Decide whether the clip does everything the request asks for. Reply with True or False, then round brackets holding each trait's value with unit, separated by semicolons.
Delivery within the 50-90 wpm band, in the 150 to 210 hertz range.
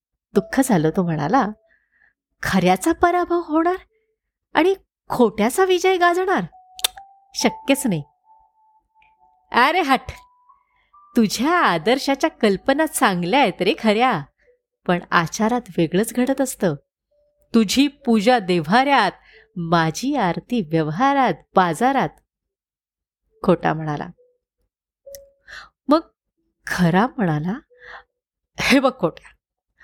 False (85 wpm; 260 Hz)